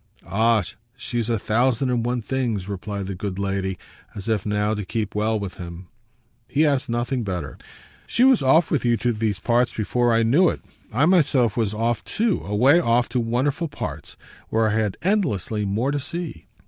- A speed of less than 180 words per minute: No, average, 185 wpm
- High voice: No, low, 115 Hz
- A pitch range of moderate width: Yes, average, 4.1 semitones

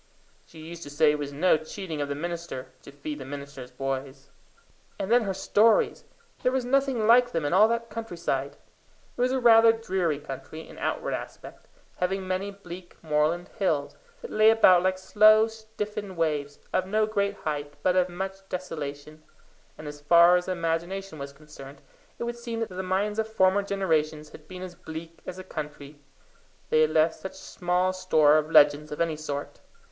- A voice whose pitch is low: No, medium, 175 Hz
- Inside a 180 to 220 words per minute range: Yes, average, 185 wpm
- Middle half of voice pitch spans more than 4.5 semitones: Yes, average, 5.0 semitones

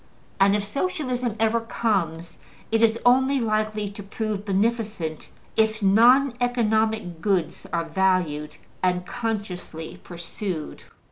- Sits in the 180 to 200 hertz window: No, high, 210 Hz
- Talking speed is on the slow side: Yes, slow, 115 wpm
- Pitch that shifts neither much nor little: Yes, average, 4.2 semitones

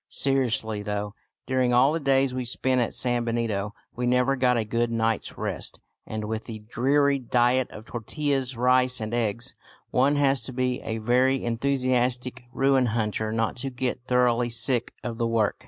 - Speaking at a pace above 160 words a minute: Yes, average, 170 wpm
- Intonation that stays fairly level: Yes, narrow, 2.1 semitones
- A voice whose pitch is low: Yes, low, 125 Hz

